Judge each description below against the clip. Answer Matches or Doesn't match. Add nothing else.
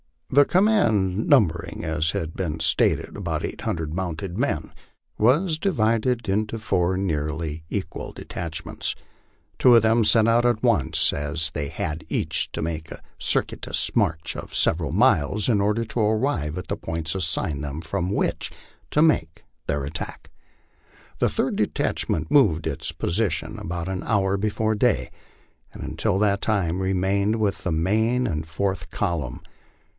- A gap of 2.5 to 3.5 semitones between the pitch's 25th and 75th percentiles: Doesn't match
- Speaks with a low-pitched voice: Matches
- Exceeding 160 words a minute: Doesn't match